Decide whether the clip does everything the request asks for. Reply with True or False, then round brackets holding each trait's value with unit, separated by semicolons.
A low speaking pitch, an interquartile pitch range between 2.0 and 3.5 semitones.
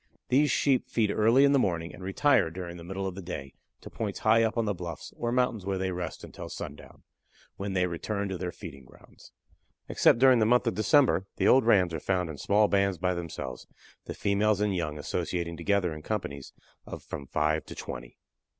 False (95 Hz; 4.3 semitones)